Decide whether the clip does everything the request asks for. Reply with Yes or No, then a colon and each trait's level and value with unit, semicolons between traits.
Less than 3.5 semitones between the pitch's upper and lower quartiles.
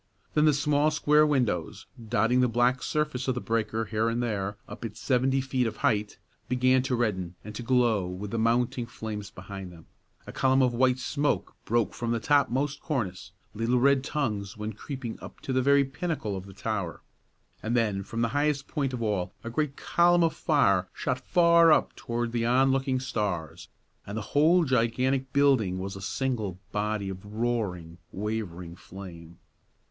No: average, 4.6 semitones